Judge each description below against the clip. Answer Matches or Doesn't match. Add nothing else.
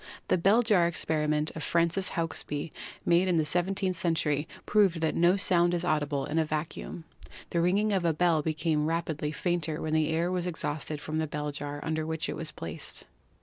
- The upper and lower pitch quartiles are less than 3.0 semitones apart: Matches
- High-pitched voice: Doesn't match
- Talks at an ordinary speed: Matches